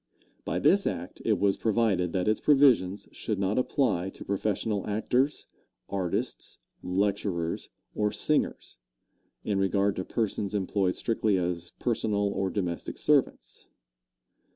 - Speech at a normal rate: No, slow, 125 wpm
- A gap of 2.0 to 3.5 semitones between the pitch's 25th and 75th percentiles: Yes, average, 2.7 semitones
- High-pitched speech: No, low, 100 Hz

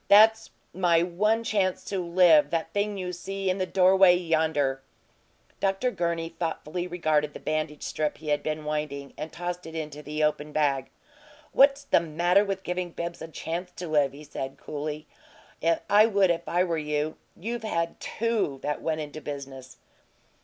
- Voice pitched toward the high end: No, medium, 170 Hz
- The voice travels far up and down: No, average, 3.7 semitones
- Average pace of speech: Yes, average, 170 wpm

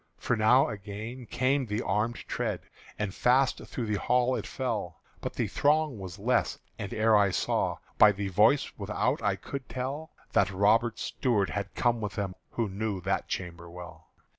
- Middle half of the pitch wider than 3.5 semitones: Yes, average, 4.0 semitones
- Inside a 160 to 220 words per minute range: Yes, average, 175 wpm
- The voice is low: Yes, low, 110 Hz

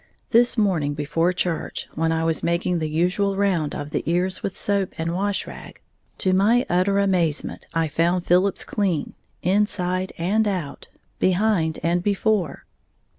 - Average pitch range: Yes, average, 3.4 semitones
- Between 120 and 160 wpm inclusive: Yes, average, 150 wpm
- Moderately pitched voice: Yes, medium, 180 Hz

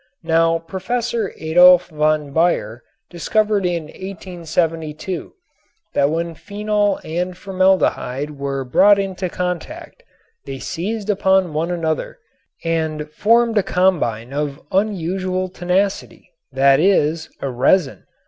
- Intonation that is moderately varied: Yes, average, 3.7 semitones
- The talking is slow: Yes, slow, 110 wpm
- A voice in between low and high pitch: Yes, medium, 175 Hz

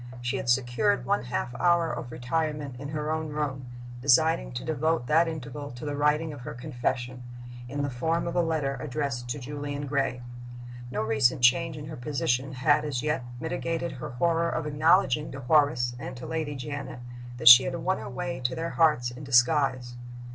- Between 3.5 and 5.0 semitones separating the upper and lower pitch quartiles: Yes, average, 3.9 semitones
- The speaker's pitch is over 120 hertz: Yes, medium, 140 Hz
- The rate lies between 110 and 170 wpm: No, average, 190 wpm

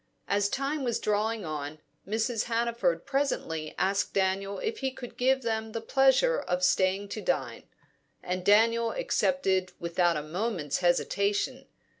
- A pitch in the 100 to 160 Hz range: No, high, 205 Hz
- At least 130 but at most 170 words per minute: Yes, average, 140 wpm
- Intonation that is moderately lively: Yes, average, 4.7 semitones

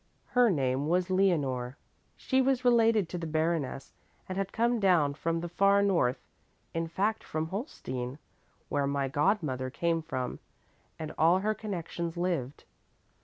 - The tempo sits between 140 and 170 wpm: Yes, average, 145 wpm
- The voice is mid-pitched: Yes, medium, 170 Hz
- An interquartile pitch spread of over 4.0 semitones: Yes, wide, 5.5 semitones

